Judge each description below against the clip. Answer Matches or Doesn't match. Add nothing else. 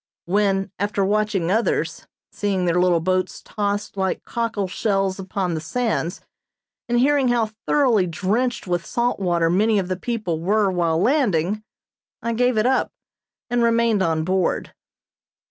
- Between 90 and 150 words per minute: Matches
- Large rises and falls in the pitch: Doesn't match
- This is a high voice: Matches